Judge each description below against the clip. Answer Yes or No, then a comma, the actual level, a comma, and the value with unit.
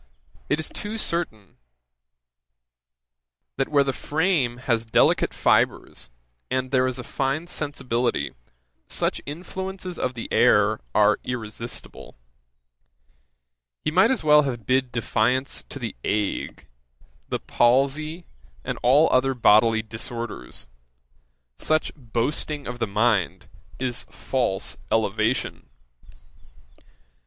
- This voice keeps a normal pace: No, slow, 110 wpm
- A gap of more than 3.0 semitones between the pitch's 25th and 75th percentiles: Yes, average, 4.5 semitones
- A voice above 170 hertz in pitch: No, low, 130 Hz